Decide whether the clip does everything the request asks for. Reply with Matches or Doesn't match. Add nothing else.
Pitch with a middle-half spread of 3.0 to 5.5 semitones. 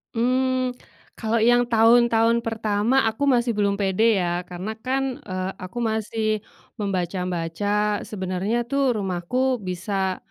Matches